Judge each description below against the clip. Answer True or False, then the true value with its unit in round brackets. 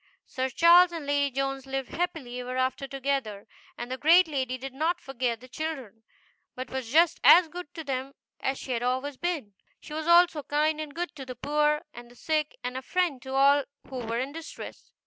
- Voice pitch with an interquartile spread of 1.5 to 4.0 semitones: True (3.5 semitones)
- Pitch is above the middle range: True (275 Hz)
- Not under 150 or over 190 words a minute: False (205 wpm)